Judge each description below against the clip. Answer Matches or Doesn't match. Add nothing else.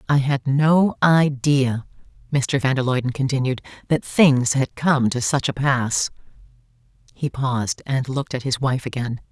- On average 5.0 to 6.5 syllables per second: Doesn't match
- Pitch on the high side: Doesn't match